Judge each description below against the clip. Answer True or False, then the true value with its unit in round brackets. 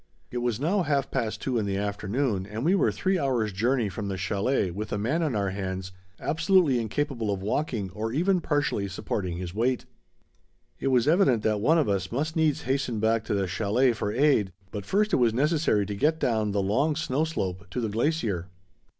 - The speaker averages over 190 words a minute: True (205 wpm)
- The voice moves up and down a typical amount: False (6.3 semitones)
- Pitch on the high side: False (115 Hz)